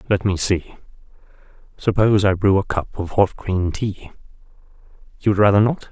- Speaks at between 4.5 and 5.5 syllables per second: Yes, 5.0 syllables/s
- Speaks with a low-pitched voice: Yes, low, 100 Hz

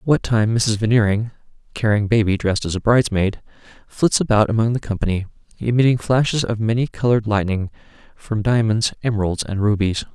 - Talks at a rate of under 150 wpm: No, average, 155 wpm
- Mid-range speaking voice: No, low, 110 Hz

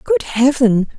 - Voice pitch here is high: Yes, high, 225 Hz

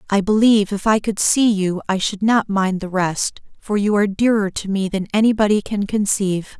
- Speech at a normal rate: No, fast, 210 wpm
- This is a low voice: No, high, 205 Hz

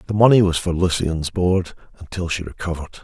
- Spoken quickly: No, average, 180 wpm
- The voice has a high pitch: No, very low, 90 Hz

